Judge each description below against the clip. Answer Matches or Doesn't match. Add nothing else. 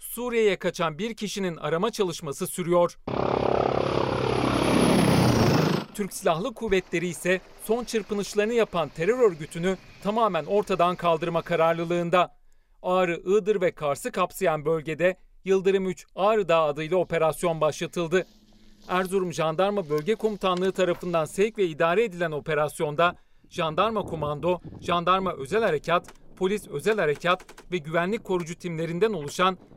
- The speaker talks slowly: Doesn't match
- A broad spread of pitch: Doesn't match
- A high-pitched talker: Doesn't match